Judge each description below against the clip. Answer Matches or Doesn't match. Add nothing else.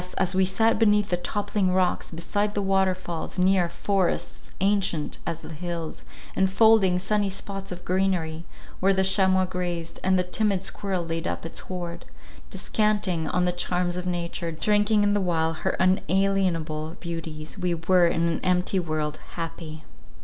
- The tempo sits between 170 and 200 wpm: Doesn't match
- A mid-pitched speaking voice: Matches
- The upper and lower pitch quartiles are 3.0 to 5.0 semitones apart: Doesn't match